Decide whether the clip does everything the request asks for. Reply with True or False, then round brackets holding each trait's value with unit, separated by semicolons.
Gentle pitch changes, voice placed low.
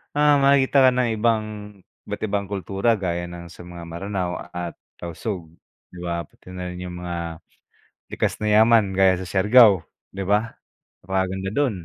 False (3.7 semitones; 95 Hz)